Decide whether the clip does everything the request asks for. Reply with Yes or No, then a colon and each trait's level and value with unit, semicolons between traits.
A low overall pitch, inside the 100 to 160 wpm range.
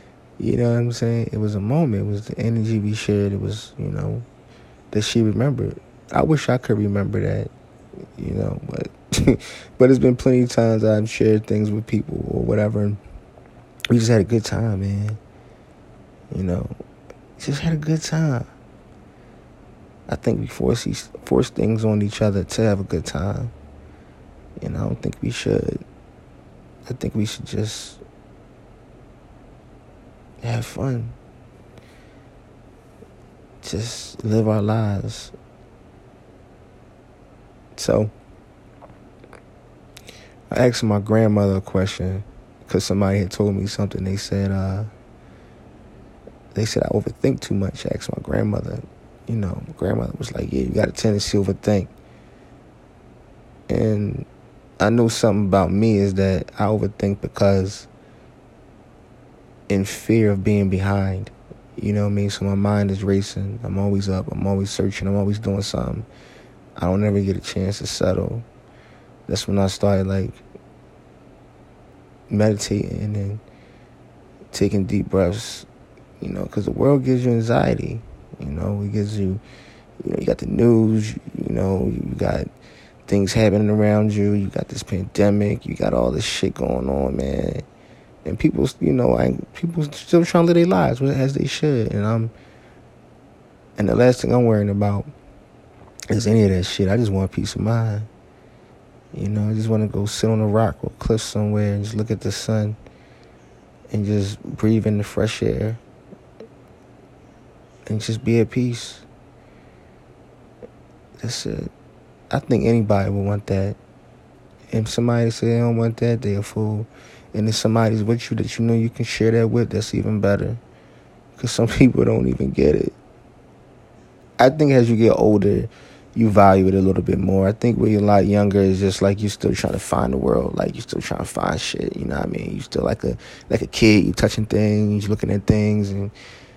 No: low, 105 Hz; average, 170 wpm